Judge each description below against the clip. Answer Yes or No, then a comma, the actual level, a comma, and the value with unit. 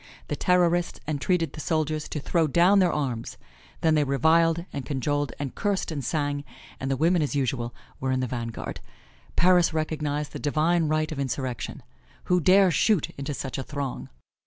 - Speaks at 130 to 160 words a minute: No, average, 175 wpm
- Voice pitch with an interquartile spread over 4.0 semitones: No, average, 3.4 semitones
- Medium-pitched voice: Yes, medium, 150 Hz